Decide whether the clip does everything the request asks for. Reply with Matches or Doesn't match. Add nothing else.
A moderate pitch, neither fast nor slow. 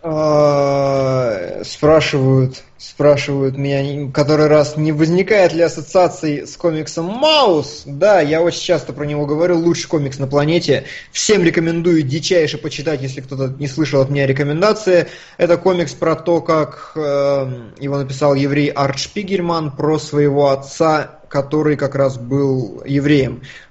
Matches